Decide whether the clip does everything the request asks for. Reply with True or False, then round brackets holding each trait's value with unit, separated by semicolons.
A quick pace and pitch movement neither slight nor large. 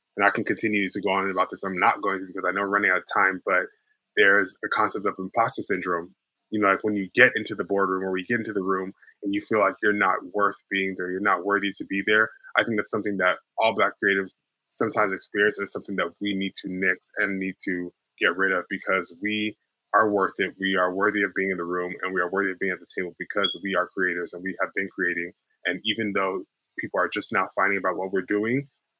False (260 wpm; 1.6 semitones)